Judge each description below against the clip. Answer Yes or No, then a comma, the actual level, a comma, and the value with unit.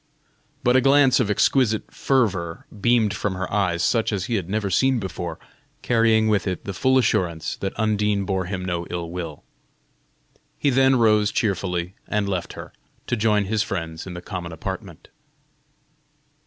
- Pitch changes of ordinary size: Yes, average, 3.8 semitones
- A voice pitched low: Yes, low, 100 Hz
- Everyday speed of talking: Yes, average, 165 wpm